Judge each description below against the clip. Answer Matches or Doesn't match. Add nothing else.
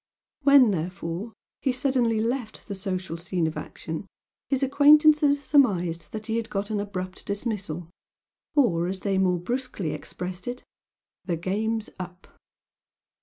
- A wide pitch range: Matches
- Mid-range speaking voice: Doesn't match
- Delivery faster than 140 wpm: Doesn't match